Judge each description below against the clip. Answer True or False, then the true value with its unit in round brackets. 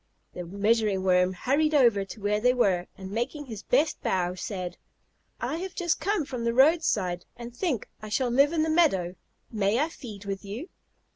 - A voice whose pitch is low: False (230 Hz)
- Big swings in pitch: True (7.0 semitones)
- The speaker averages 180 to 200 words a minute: True (190 wpm)